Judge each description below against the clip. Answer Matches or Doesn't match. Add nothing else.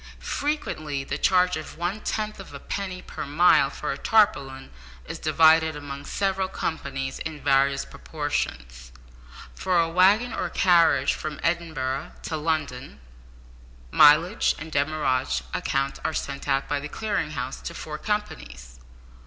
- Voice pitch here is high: Doesn't match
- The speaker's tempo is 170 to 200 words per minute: Doesn't match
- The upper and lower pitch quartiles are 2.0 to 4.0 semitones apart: Doesn't match